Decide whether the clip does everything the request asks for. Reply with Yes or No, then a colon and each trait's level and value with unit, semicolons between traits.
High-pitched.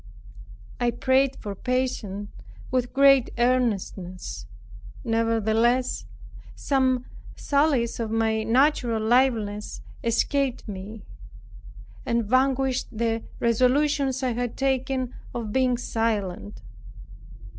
Yes: high, 240 Hz